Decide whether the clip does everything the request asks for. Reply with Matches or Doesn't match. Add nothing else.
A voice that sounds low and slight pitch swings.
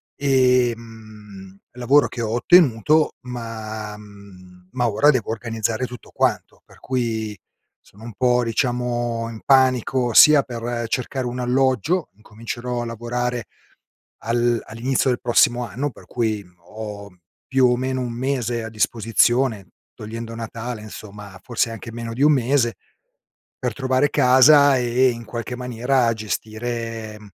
Matches